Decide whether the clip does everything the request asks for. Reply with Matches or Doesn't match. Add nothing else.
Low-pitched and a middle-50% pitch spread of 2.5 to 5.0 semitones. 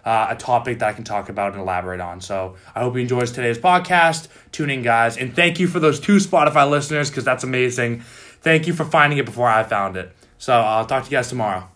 Doesn't match